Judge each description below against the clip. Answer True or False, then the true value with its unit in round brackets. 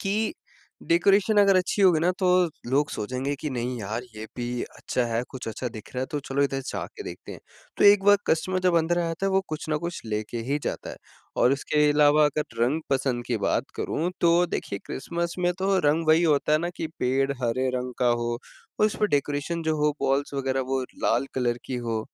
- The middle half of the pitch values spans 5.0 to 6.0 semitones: True (5.4 semitones)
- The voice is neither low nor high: True (145 Hz)